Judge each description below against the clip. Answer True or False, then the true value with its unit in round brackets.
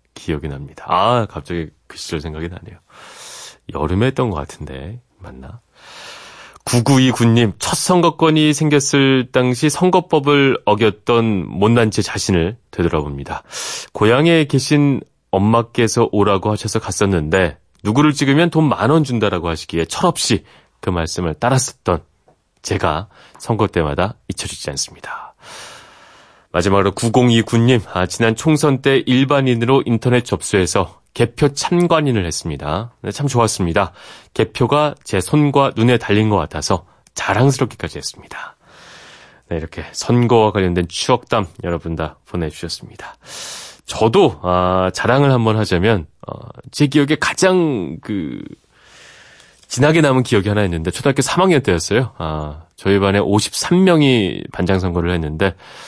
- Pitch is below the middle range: True (110 Hz)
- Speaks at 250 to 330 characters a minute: True (295 characters per minute)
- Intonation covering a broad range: True (7.2 semitones)